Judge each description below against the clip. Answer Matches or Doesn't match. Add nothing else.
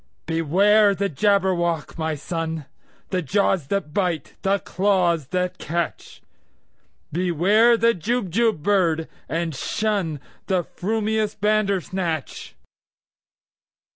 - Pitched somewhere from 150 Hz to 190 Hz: Matches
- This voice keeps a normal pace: Doesn't match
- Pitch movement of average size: Matches